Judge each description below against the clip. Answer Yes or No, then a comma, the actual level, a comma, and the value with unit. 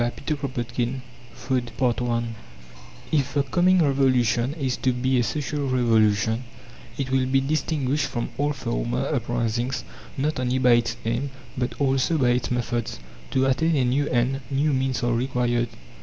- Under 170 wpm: Yes, average, 155 wpm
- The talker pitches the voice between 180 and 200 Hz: No, low, 130 Hz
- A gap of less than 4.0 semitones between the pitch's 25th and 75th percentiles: Yes, narrow, 2.4 semitones